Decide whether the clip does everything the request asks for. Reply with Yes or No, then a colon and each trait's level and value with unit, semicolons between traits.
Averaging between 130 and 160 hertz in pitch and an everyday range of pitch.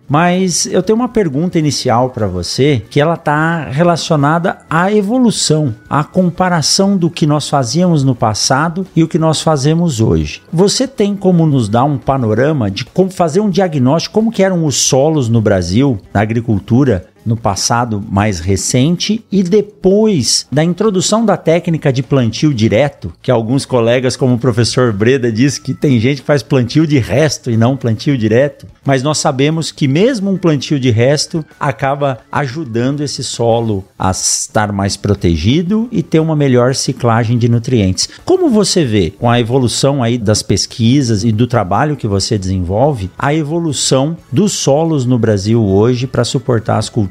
No: medium, 140 Hz; wide, 6.0 semitones